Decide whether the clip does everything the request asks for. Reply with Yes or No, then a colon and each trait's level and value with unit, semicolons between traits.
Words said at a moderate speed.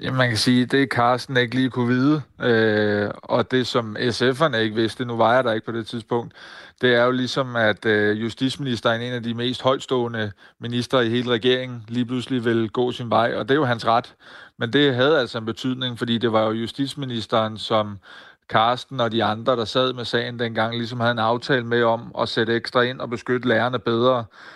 Yes: average, 215 wpm